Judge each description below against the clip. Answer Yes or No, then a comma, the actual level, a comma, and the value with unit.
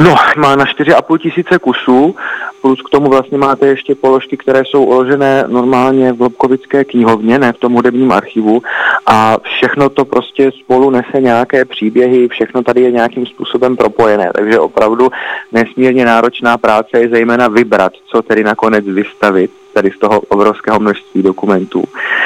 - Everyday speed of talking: Yes, average, 155 wpm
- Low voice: Yes, low, 125 Hz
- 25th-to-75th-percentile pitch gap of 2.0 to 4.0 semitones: Yes, narrow, 2.6 semitones